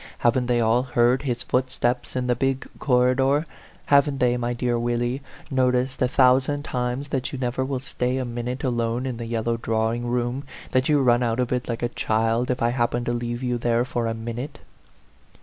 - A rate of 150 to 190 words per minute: No, average, 200 wpm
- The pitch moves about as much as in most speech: No, narrow, 1.4 semitones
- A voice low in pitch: Yes, low, 125 Hz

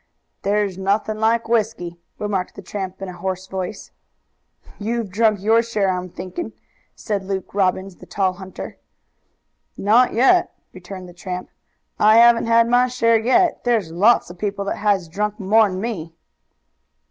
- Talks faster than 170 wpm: No, average, 150 wpm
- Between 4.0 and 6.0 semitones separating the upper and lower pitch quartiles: No, average, 3.4 semitones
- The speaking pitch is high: Yes, high, 205 Hz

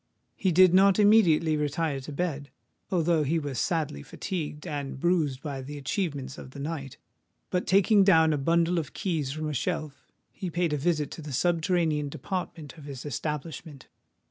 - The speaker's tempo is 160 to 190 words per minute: Yes, average, 170 wpm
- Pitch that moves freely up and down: No, average, 3.4 semitones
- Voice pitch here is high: No, medium, 155 Hz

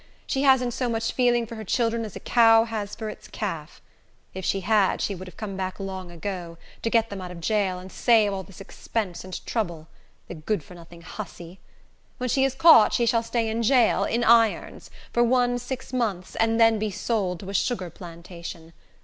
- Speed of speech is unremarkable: No, fast, 210 wpm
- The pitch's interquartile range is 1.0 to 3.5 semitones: No, average, 4.1 semitones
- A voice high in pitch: Yes, high, 215 Hz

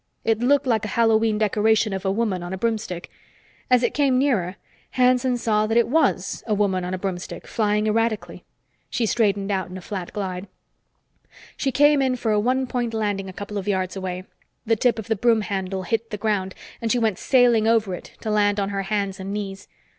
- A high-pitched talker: Yes, high, 215 Hz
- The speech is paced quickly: Yes, fast, 210 wpm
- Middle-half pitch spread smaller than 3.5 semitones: Yes, average, 3.1 semitones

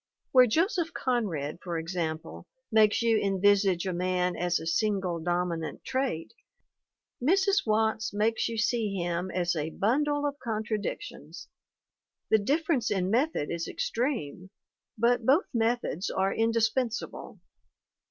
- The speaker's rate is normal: No, slow, 125 wpm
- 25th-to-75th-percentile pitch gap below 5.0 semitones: No, wide, 5.4 semitones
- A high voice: Yes, high, 215 Hz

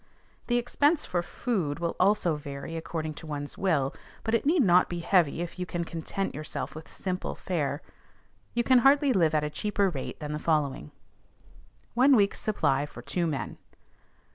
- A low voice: No, medium, 170 Hz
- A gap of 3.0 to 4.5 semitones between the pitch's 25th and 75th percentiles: No, wide, 5.5 semitones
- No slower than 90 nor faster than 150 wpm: No, average, 175 wpm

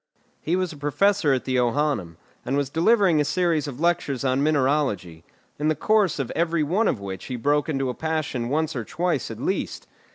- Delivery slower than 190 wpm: No, average, 195 wpm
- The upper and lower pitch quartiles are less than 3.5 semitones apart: No, average, 4.1 semitones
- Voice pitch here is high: No, medium, 145 Hz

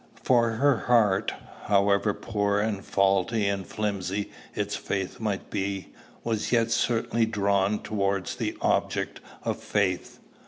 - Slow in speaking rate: Yes, slow, 125 wpm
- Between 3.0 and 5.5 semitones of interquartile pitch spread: No, narrow, 2.4 semitones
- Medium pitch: No, low, 100 Hz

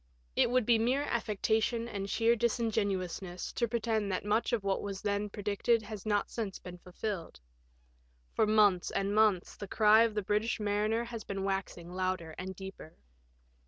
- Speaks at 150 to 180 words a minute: Yes, average, 170 wpm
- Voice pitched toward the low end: No, high, 210 Hz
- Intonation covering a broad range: No, narrow, 2.6 semitones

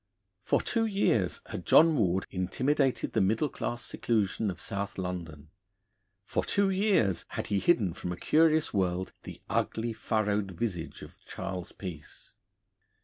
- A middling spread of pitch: No, wide, 6.6 semitones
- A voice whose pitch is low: Yes, low, 100 Hz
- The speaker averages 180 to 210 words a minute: No, average, 145 wpm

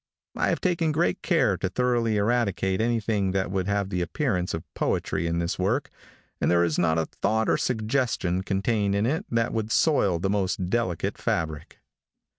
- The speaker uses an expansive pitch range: No, average, 4.4 semitones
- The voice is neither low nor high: No, low, 100 Hz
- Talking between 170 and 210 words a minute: Yes, average, 180 wpm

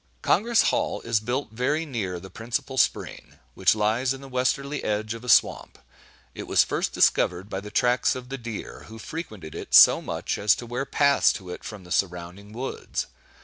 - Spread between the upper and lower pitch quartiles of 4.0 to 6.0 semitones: Yes, average, 4.5 semitones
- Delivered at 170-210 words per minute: Yes, average, 190 wpm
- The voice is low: Yes, low, 115 Hz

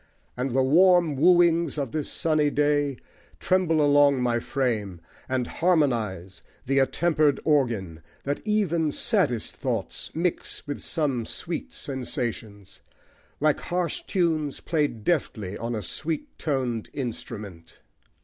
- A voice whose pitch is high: No, medium, 145 Hz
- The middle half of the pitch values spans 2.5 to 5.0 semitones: No, wide, 5.4 semitones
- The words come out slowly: Yes, slow, 120 wpm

